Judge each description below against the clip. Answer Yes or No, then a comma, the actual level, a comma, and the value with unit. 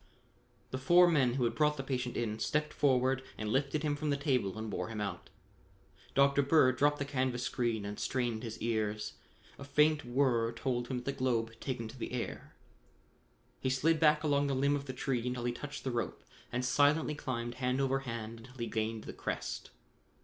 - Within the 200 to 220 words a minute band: Yes, fast, 205 wpm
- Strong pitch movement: No, average, 3.3 semitones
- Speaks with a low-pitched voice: Yes, low, 130 Hz